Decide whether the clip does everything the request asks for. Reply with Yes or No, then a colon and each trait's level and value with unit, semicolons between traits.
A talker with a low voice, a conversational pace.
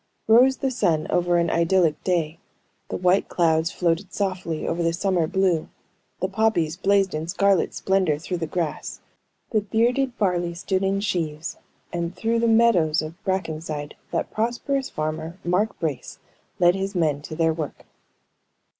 No: medium, 175 Hz; average, 155 wpm